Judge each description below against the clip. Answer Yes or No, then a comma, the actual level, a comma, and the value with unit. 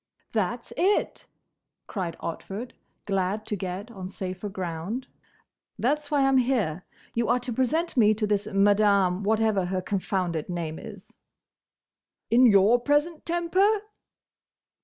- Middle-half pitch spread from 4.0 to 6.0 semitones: Yes, average, 5.0 semitones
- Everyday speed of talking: No, slow, 125 wpm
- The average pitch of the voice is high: Yes, high, 210 Hz